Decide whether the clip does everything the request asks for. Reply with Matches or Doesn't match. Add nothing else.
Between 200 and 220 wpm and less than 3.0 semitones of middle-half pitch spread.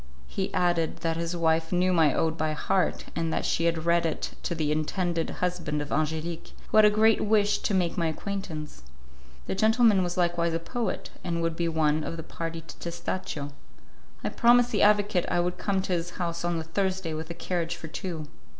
Matches